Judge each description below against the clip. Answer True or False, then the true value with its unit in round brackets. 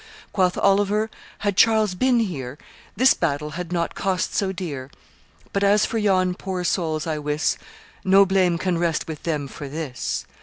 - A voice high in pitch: False (180 Hz)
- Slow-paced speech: False (165 wpm)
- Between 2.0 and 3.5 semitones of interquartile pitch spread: False (4.1 semitones)